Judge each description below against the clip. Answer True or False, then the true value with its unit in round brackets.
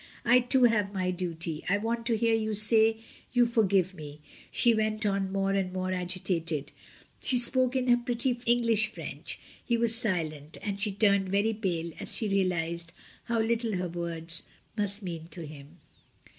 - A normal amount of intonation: True (4.6 semitones)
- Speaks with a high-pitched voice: True (200 Hz)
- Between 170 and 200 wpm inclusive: True (175 wpm)